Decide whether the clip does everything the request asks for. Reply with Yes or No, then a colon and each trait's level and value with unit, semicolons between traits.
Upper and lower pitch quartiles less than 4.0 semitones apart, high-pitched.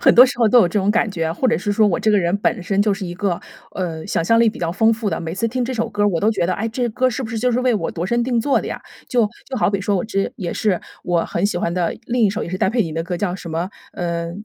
No: average, 4.6 semitones; high, 205 Hz